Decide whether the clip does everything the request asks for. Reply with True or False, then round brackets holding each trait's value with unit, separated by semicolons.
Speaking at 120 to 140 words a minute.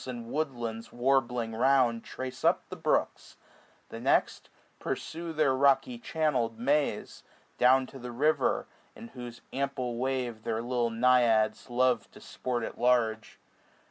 True (135 wpm)